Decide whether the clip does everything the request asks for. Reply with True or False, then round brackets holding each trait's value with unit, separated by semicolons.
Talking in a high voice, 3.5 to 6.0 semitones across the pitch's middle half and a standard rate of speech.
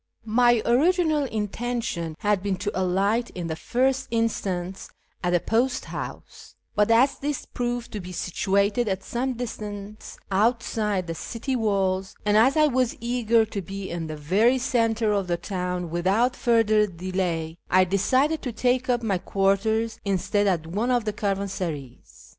True (210 Hz; 4.3 semitones; 160 wpm)